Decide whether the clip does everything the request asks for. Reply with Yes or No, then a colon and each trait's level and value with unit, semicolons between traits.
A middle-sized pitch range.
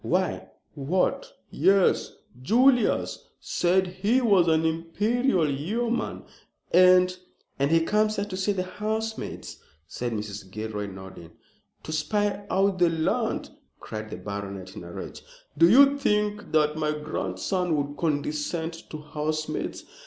No: wide, 6.1 semitones